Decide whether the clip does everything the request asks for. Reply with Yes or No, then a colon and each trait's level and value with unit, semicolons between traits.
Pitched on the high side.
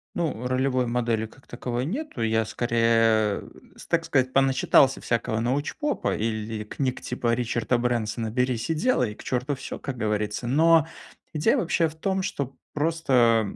No: low, 125 Hz